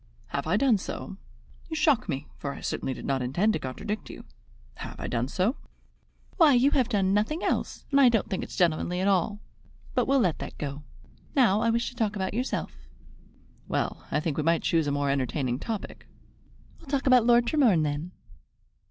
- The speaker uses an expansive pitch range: Yes, wide, 8.0 semitones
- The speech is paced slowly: No, average, 185 wpm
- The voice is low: No, high, 200 Hz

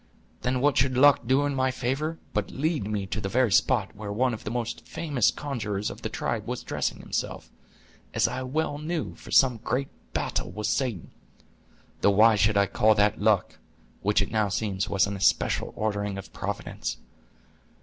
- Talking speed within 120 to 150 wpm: No, average, 180 wpm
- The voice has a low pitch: Yes, low, 110 Hz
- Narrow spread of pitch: No, average, 4.3 semitones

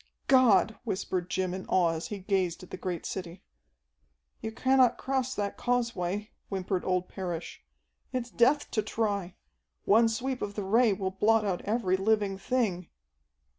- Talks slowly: No, average, 155 wpm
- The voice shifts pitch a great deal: No, average, 3.9 semitones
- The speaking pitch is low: No, high, 200 Hz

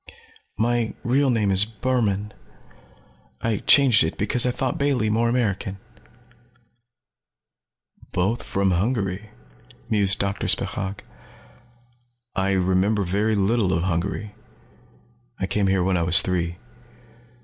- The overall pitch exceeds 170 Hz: No, low, 100 Hz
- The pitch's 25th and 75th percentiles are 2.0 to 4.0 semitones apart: Yes, average, 3.2 semitones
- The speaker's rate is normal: No, slow, 115 wpm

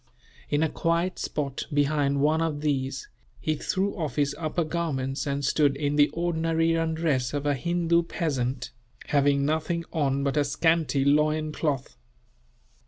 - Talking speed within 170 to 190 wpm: No, average, 145 wpm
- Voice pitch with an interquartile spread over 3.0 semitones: No, average, 2.7 semitones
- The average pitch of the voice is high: No, medium, 150 Hz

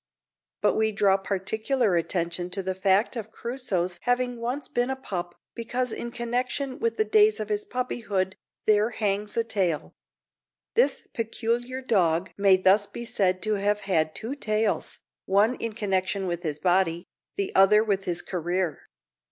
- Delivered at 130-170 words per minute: Yes, average, 160 wpm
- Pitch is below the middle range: No, high, 210 Hz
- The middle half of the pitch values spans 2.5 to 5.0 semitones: Yes, average, 4.2 semitones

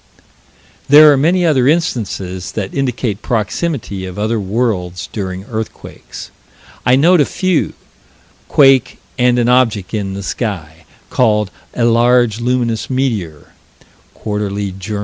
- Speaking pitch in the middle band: No, low, 115 Hz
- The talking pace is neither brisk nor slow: No, slow, 125 wpm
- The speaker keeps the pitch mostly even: No, average, 4.4 semitones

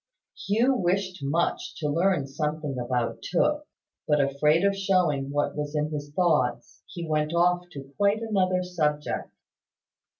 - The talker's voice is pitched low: No, medium, 160 Hz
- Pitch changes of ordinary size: Yes, average, 4.2 semitones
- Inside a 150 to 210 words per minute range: No, average, 140 wpm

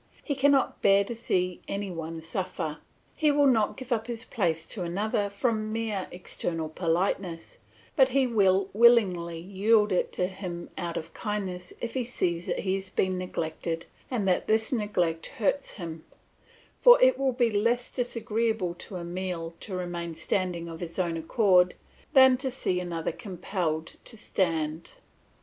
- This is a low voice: No, high, 190 Hz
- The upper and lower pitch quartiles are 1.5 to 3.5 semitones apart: No, average, 4.8 semitones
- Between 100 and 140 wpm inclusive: No, average, 160 wpm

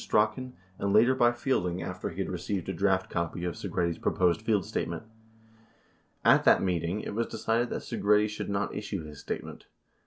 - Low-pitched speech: Yes, very low, 95 Hz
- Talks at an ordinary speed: Yes, average, 175 wpm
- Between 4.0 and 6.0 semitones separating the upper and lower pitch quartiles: No, average, 3.3 semitones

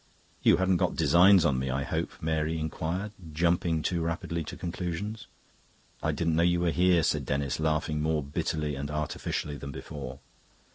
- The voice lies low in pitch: Yes, very low, 80 Hz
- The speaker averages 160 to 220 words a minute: Yes, average, 170 wpm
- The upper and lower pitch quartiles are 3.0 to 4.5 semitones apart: No, narrow, 2.4 semitones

